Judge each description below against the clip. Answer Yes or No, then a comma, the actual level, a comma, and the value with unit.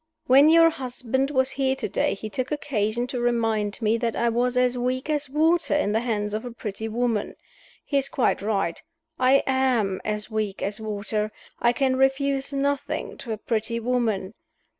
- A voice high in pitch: Yes, high, 245 Hz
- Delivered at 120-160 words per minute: No, average, 180 wpm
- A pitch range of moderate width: Yes, average, 3.7 semitones